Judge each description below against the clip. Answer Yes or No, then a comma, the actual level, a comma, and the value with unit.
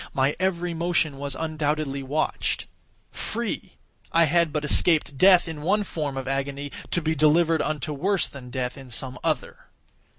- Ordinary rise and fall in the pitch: Yes, average, 3.4 semitones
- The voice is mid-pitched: Yes, medium, 150 Hz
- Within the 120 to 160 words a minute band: Yes, average, 155 wpm